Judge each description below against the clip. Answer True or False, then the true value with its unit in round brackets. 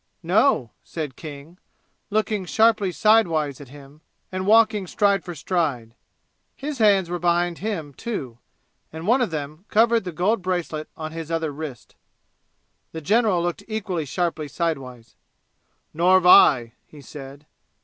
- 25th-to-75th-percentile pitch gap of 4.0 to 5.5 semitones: True (5.2 semitones)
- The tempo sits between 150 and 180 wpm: False (140 wpm)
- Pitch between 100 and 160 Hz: False (170 Hz)